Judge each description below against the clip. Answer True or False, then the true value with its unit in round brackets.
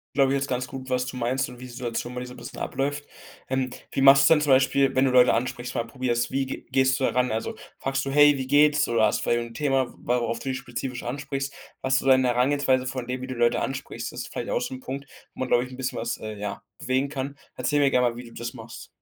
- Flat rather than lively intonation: True (1.7 semitones)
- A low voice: True (130 Hz)